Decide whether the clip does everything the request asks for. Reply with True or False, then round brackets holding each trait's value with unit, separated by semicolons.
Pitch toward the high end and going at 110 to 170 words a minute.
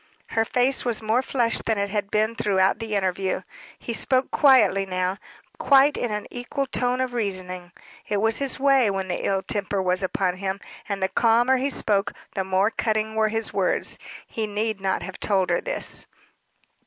False (215 Hz; 185 wpm)